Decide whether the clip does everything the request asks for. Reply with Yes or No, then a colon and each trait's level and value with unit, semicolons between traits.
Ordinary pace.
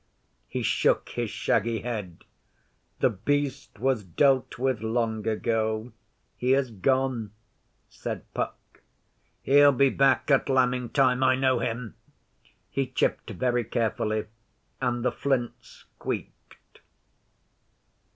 No: slow, 110 wpm